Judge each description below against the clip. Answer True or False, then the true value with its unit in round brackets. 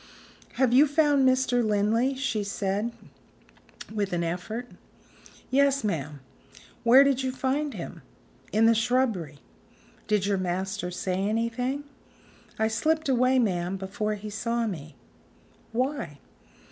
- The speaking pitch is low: False (225 Hz)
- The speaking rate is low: True (120 wpm)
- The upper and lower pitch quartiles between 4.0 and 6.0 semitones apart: True (5.1 semitones)